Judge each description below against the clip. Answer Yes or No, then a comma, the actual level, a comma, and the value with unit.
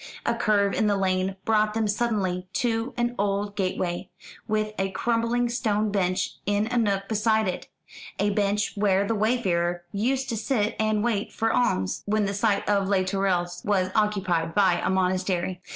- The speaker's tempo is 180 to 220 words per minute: No, average, 170 wpm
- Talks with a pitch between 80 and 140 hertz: No, high, 205 Hz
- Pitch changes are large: No, narrow, 2.6 semitones